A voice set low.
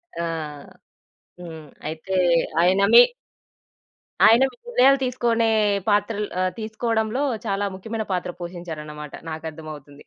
No: high, 190 Hz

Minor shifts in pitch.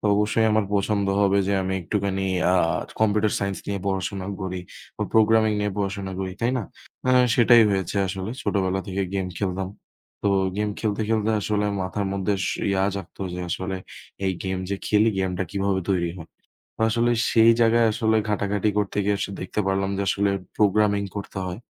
Yes: narrow, 1.8 semitones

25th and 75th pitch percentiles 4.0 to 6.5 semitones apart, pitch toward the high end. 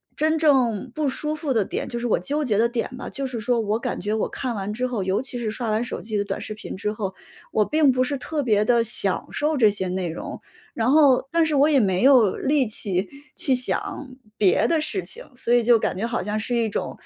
Yes: average, 4.5 semitones; high, 235 Hz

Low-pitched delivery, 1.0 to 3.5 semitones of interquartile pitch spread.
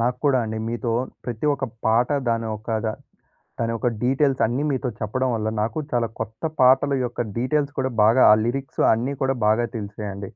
Yes: low, 120 Hz; average, 2.9 semitones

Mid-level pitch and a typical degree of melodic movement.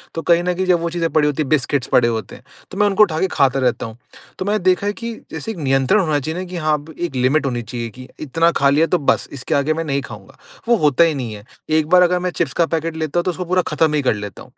Yes: medium, 155 Hz; average, 4.5 semitones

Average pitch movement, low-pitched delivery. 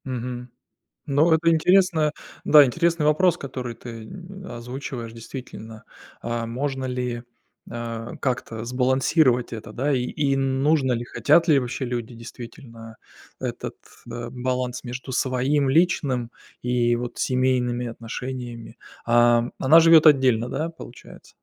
Yes: average, 3.2 semitones; low, 125 Hz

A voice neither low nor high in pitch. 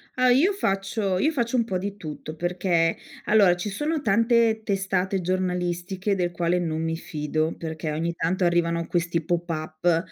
Yes: medium, 180 Hz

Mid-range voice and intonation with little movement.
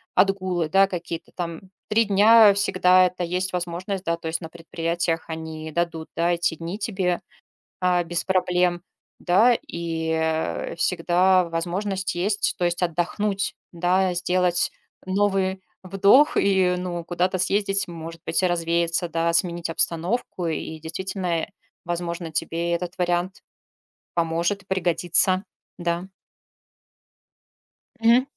Yes: medium, 175 Hz; narrow, 2.1 semitones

